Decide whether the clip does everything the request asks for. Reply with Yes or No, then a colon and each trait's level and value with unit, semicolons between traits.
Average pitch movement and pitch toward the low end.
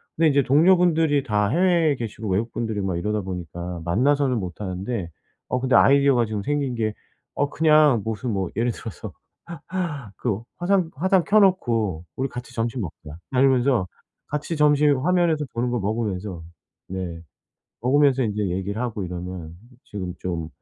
No: wide, 6.9 semitones; low, 120 Hz